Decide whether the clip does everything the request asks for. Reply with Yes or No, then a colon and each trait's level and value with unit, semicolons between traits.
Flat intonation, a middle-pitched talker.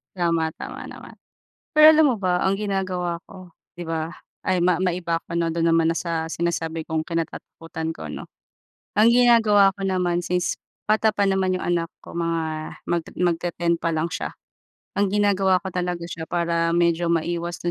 Yes: narrow, 2.1 semitones; medium, 175 Hz